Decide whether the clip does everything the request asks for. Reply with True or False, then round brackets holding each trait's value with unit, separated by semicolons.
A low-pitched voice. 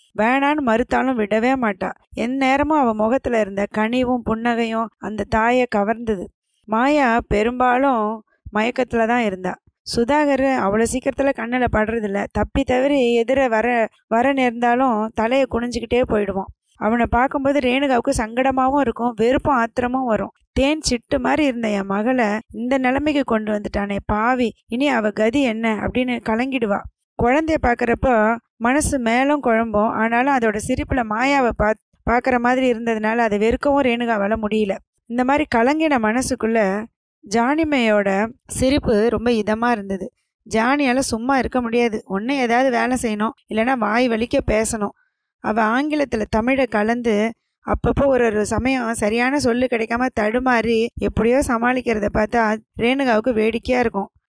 False (235 Hz)